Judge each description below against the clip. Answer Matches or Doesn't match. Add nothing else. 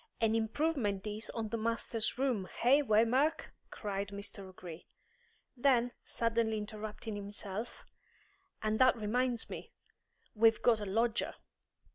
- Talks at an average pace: Doesn't match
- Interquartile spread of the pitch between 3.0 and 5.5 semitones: Doesn't match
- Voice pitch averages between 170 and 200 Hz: Doesn't match